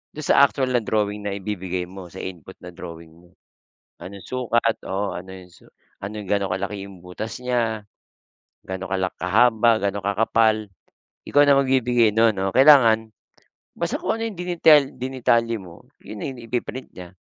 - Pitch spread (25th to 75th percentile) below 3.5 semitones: No, average, 4.5 semitones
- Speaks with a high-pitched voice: No, low, 105 Hz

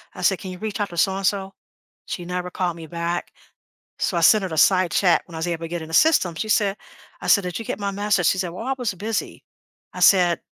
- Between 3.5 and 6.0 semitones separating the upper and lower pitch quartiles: No, average, 2.7 semitones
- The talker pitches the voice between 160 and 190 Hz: Yes, medium, 185 Hz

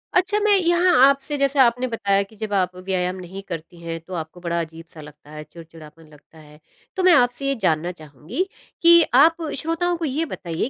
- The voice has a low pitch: No, high, 195 Hz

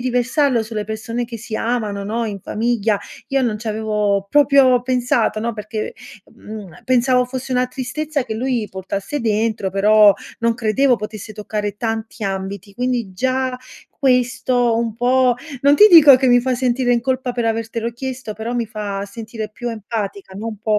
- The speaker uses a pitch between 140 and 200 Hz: No, high, 230 Hz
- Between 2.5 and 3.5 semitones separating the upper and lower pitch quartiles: Yes, average, 2.9 semitones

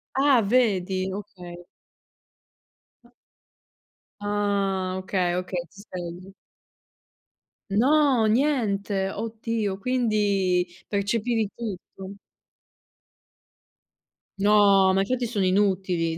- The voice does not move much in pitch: No, average, 3.0 semitones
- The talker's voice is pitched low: No, high, 200 Hz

